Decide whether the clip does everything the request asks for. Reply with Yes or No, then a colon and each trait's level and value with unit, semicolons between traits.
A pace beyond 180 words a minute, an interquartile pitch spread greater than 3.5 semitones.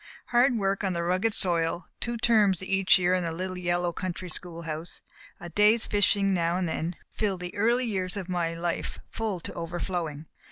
No: average, 190 wpm; average, 2.9 semitones